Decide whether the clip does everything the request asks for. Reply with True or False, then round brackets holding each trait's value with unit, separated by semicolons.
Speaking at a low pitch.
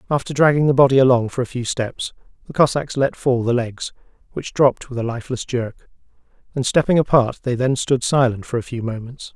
True (125 Hz)